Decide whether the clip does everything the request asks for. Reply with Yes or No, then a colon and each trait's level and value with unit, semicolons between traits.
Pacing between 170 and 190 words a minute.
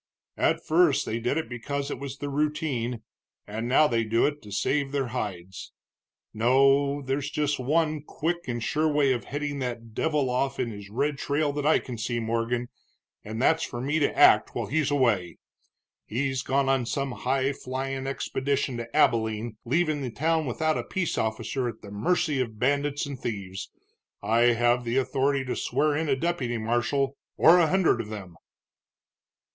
Yes: average, 180 wpm